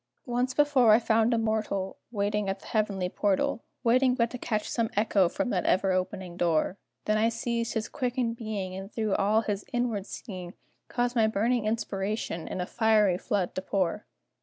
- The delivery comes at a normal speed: Yes, average, 185 wpm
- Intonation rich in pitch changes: No, average, 3.3 semitones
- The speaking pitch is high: Yes, high, 215 Hz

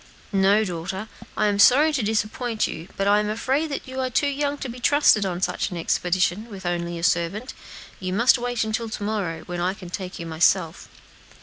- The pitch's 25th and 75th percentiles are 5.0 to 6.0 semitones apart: Yes, average, 5.3 semitones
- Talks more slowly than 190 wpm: No, fast, 205 wpm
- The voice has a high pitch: Yes, high, 205 Hz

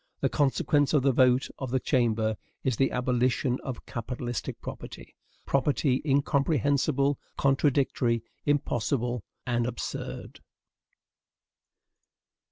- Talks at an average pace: No, slow, 95 wpm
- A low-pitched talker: Yes, low, 130 Hz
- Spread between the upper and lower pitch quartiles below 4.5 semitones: Yes, narrow, 2.5 semitones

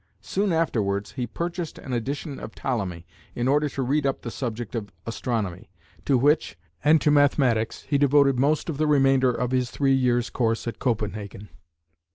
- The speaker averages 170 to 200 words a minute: Yes, average, 175 wpm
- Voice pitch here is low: Yes, low, 130 Hz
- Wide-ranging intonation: No, average, 3.9 semitones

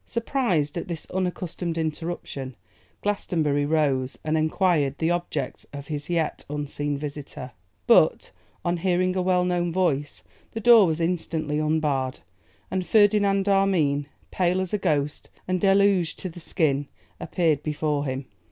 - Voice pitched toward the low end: No, medium, 165 Hz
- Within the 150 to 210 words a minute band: No, average, 140 wpm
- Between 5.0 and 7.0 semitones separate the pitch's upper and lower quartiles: No, average, 3.9 semitones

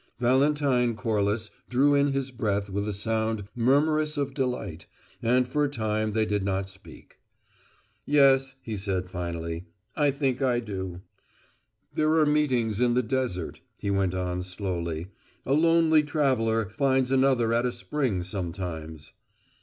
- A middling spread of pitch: No, wide, 5.8 semitones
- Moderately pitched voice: No, low, 115 Hz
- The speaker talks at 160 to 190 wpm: No, average, 145 wpm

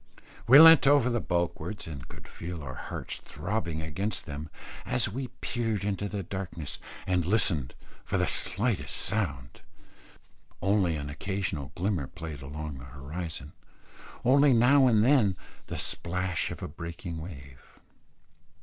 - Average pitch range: No, wide, 5.9 semitones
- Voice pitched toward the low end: Yes, very low, 90 Hz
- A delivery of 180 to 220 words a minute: No, average, 140 wpm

